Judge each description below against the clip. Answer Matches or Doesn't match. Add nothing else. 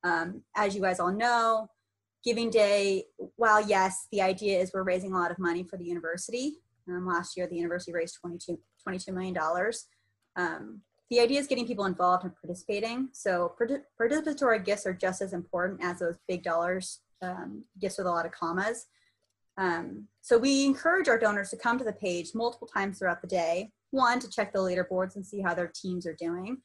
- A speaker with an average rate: Matches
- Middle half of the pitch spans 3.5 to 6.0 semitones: Matches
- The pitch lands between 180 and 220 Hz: Matches